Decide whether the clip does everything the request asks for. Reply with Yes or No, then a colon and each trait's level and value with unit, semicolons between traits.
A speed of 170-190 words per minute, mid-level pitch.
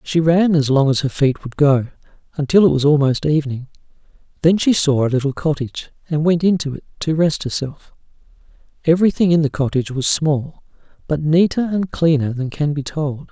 Yes: average, 185 wpm; medium, 150 Hz